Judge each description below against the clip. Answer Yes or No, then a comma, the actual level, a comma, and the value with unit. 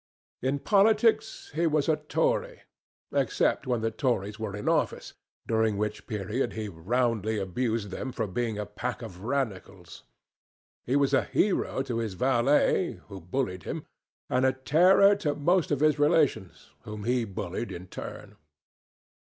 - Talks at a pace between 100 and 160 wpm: Yes, average, 150 wpm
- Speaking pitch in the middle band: No, low, 120 Hz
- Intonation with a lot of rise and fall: Yes, wide, 5.8 semitones